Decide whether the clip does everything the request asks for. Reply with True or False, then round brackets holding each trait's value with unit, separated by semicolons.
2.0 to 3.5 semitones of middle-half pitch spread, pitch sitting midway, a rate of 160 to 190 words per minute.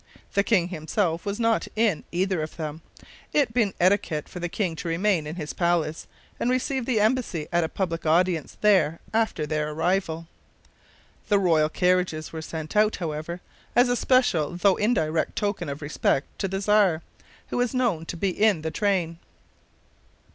False (4.5 semitones; 180 Hz; 170 wpm)